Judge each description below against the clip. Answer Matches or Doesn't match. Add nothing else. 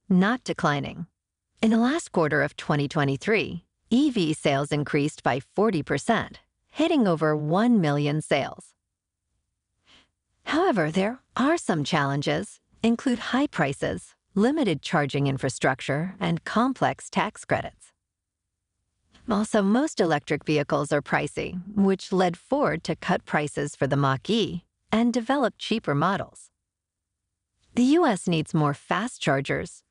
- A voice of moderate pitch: Matches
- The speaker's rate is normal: Doesn't match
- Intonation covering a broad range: Matches